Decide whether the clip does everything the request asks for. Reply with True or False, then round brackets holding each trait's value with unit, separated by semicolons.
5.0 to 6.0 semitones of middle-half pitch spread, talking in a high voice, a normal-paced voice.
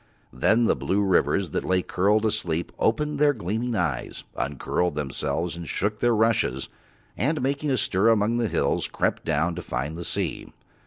False (5.4 semitones; 105 Hz; 170 wpm)